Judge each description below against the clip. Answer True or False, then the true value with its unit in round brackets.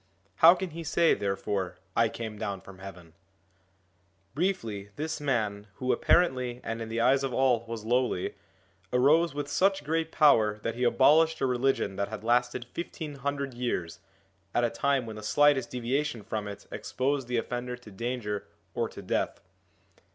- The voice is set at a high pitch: False (120 Hz)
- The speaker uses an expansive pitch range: False (4.9 semitones)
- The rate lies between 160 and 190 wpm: True (170 wpm)